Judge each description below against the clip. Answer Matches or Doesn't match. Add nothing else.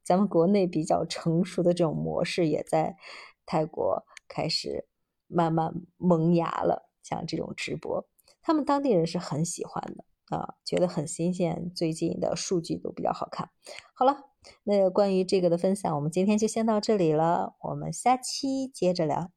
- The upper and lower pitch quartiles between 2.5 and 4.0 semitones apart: Matches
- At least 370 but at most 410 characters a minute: Doesn't match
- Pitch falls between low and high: Matches